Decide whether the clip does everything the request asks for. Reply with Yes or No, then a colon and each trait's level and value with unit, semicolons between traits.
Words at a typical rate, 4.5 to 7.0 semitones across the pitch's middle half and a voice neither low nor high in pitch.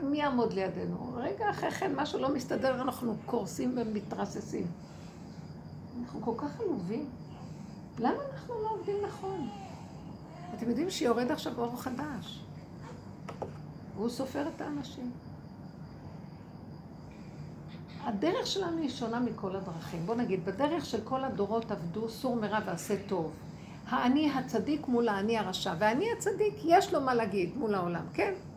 No: average, 130 wpm; wide, 5.5 semitones; high, 235 Hz